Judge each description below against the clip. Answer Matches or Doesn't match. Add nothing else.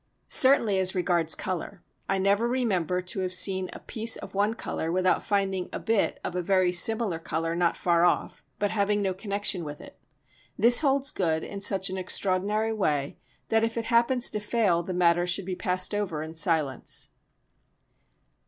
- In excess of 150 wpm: Matches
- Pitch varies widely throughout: Doesn't match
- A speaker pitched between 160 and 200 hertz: Matches